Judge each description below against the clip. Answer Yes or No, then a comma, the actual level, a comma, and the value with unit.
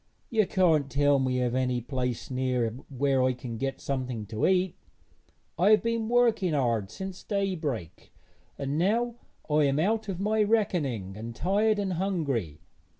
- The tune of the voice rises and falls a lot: Yes, wide, 7.6 semitones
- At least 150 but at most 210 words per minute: Yes, average, 155 wpm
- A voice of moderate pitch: Yes, medium, 145 Hz